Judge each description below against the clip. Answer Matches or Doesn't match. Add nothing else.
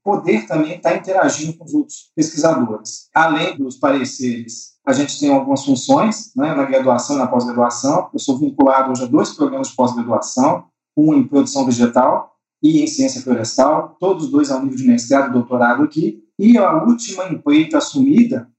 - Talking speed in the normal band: Matches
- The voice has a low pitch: Doesn't match